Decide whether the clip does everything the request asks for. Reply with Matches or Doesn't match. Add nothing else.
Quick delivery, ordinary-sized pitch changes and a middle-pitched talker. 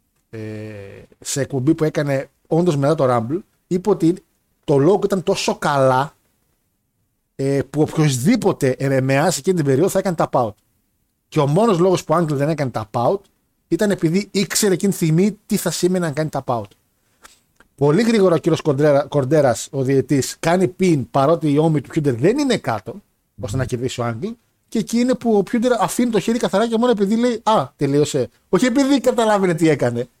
Doesn't match